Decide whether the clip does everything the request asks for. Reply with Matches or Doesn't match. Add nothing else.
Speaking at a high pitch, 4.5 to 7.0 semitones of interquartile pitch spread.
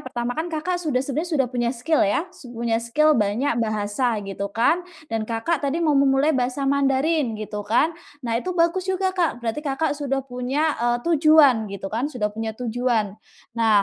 Matches